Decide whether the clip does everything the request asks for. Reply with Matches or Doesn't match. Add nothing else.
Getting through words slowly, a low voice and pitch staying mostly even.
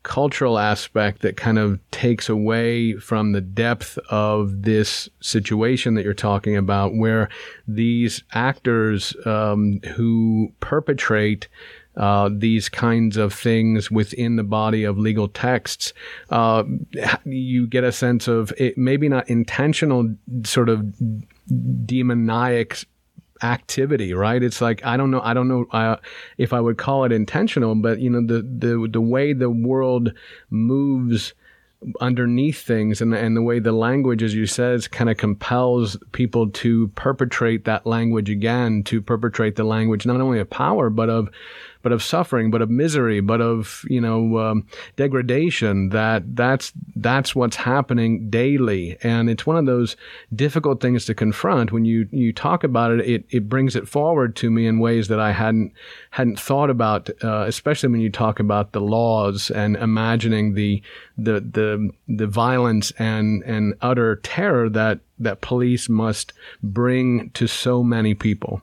Doesn't match